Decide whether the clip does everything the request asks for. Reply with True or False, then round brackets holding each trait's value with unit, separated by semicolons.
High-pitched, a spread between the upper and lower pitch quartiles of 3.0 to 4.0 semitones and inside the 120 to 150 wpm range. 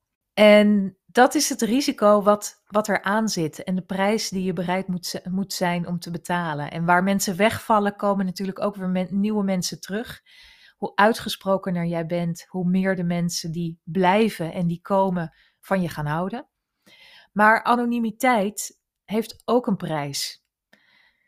False (195 Hz; 3.4 semitones; 160 wpm)